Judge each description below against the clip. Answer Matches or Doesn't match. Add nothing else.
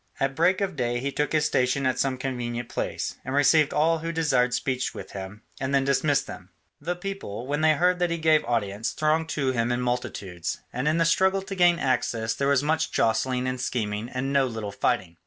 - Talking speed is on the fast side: Matches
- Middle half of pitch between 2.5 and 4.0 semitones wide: Doesn't match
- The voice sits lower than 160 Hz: Matches